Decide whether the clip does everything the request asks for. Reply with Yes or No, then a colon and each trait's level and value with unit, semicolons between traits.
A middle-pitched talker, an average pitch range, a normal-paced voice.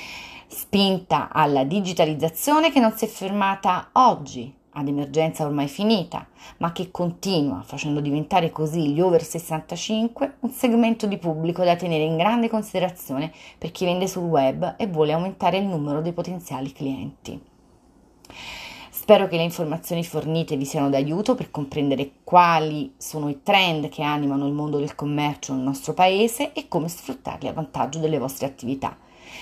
Yes: medium, 165 Hz; average, 4.4 semitones; average, 155 wpm